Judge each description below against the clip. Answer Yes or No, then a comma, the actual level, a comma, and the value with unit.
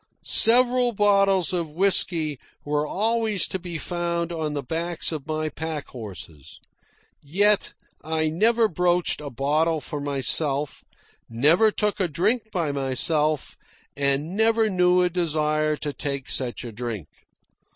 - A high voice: No, medium, 160 Hz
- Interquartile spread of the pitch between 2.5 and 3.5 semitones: No, average, 4.6 semitones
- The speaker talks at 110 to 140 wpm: Yes, slow, 135 wpm